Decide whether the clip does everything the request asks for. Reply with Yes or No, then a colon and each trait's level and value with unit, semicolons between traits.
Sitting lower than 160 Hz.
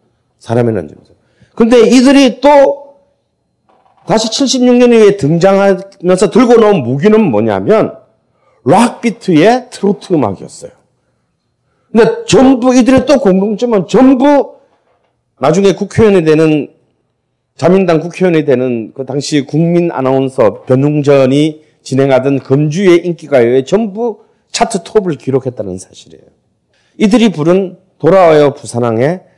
No: medium, 185 Hz